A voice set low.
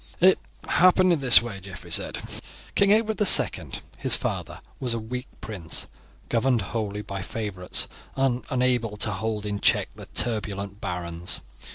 Yes: low, 110 Hz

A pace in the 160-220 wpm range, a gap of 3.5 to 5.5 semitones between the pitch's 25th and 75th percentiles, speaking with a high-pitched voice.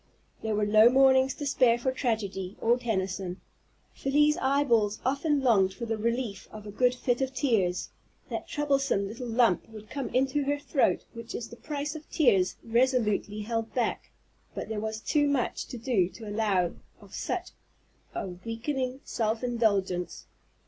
Yes: average, 165 wpm; average, 4.1 semitones; high, 235 Hz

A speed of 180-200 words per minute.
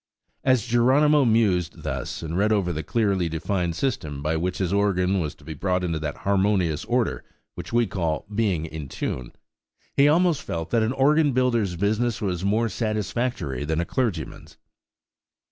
No: average, 165 wpm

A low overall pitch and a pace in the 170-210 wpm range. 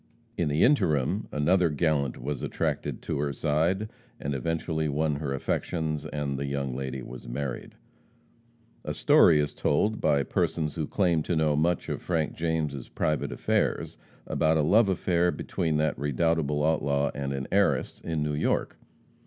No: very low, 75 Hz; average, 160 wpm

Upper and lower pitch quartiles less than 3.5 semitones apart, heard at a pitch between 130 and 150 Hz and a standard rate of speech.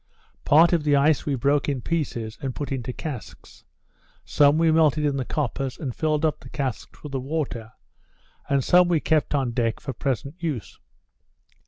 Yes: average, 3.0 semitones; medium, 140 Hz; average, 180 wpm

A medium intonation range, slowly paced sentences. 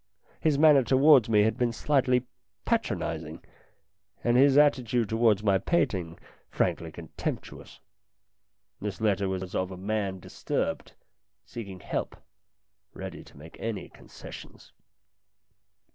Yes: average, 5.0 semitones; slow, 115 wpm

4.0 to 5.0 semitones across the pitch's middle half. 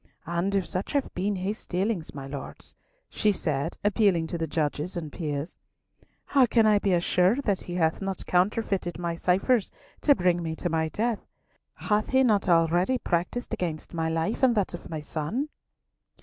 Yes: average, 4.3 semitones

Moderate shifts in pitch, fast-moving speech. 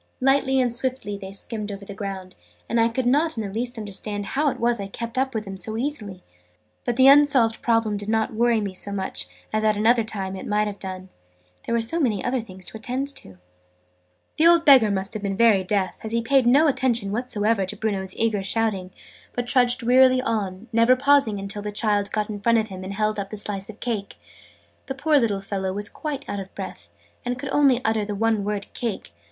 Yes: average, 3.7 semitones; fast, 225 wpm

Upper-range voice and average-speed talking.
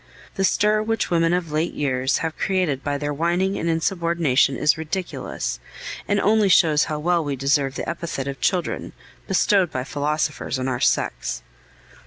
No: medium, 160 Hz; average, 165 wpm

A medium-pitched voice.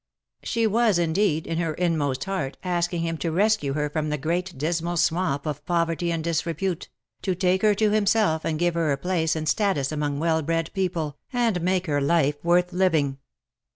Yes: medium, 170 Hz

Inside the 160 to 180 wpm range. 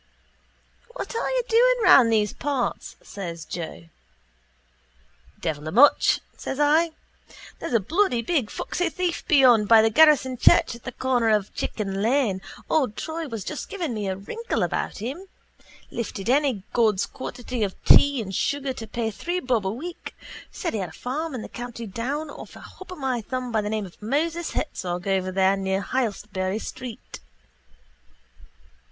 Yes: average, 165 wpm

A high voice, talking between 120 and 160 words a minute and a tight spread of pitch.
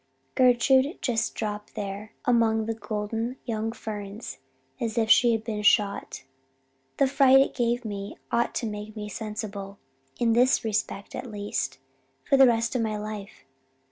Yes: high, 220 Hz; average, 155 wpm; narrow, 2.3 semitones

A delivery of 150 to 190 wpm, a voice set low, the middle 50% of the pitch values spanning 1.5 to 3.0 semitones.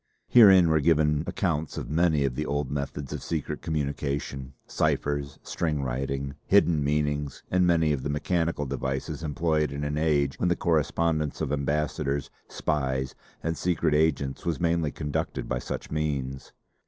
Yes: average, 155 wpm; very low, 75 Hz; narrow, 2.5 semitones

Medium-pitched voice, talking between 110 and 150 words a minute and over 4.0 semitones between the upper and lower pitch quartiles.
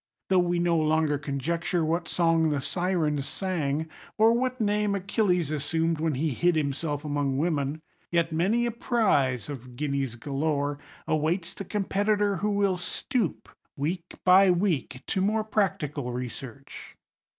Yes: medium, 165 Hz; average, 140 wpm; average, 4.9 semitones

